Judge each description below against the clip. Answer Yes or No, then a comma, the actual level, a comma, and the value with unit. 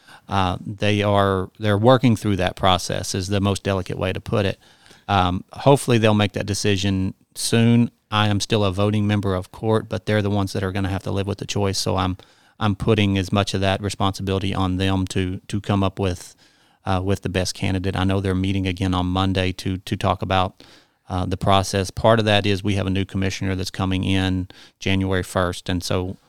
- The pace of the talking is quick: Yes, fast, 220 wpm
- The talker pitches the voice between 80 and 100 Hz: Yes, very low, 95 Hz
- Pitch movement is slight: Yes, narrow, 1.6 semitones